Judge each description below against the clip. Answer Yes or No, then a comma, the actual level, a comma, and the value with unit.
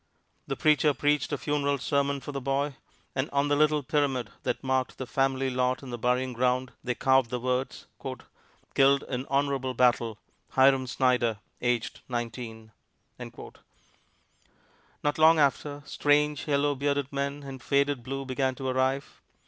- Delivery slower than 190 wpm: Yes, average, 150 wpm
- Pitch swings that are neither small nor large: No, narrow, 1.9 semitones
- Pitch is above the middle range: No, low, 135 Hz